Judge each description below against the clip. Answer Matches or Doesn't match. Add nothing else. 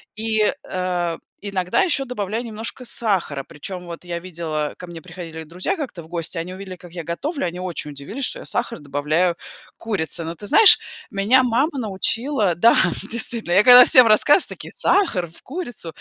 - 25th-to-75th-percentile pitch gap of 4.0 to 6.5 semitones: Matches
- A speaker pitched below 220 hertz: Matches